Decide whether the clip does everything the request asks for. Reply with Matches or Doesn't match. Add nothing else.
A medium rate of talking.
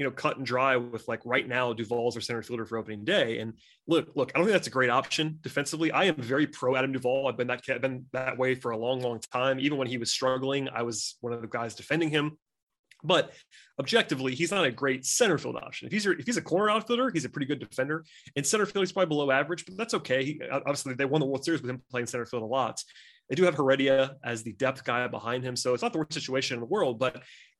Doesn't match